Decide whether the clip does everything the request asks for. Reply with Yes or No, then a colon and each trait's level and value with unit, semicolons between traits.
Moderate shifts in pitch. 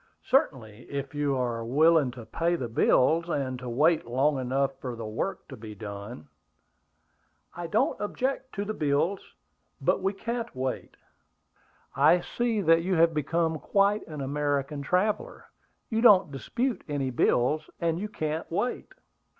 No: wide, 5.9 semitones